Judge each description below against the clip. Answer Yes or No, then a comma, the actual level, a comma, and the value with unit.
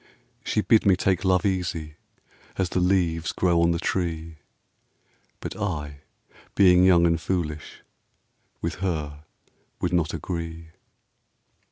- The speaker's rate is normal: No, slow, 125 wpm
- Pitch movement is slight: Yes, narrow, 2.3 semitones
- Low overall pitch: Yes, very low, 85 Hz